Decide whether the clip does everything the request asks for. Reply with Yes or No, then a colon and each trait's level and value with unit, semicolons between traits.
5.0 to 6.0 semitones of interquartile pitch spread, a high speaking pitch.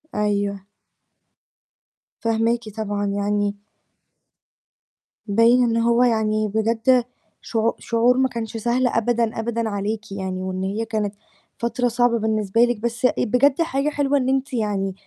No: average, 2.7 semitones; high, 225 Hz